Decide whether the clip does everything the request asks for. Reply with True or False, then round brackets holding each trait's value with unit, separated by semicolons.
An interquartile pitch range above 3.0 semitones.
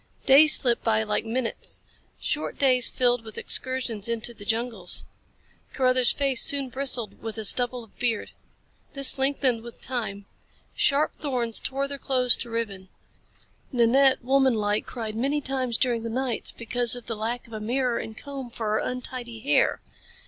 False (2.7 semitones)